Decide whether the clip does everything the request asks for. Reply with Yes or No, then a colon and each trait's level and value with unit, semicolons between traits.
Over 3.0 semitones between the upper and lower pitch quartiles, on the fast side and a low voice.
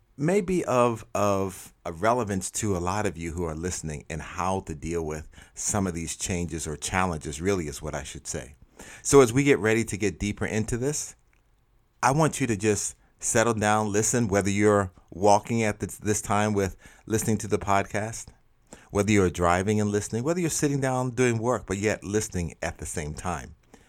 No: average, 4.1 semitones; average, 195 wpm; low, 105 Hz